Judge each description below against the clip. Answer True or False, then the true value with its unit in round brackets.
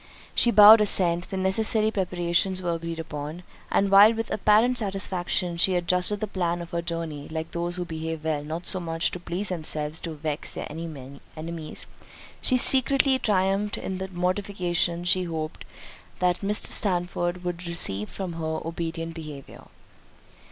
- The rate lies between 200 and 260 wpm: False (160 wpm)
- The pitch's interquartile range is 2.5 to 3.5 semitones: True (2.8 semitones)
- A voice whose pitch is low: False (175 Hz)